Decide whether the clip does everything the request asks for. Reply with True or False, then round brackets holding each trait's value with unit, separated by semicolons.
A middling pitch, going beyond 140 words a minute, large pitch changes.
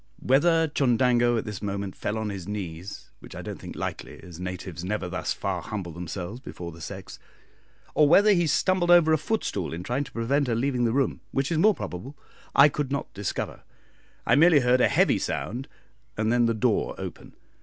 False (120 Hz; 195 wpm; 6.5 semitones)